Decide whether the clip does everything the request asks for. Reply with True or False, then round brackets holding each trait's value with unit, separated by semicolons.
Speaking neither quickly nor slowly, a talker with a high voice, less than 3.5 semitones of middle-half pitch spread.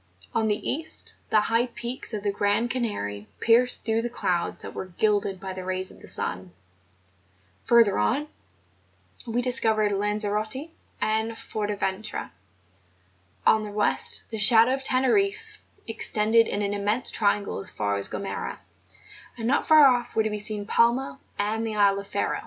True (160 wpm; 215 Hz; 2.6 semitones)